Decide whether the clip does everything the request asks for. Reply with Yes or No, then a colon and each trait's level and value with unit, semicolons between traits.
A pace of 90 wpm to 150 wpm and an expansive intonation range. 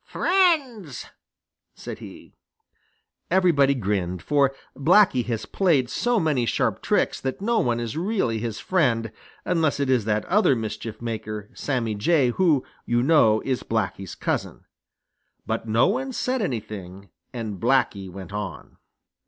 Yes: slow, 135 wpm; wide, 7.6 semitones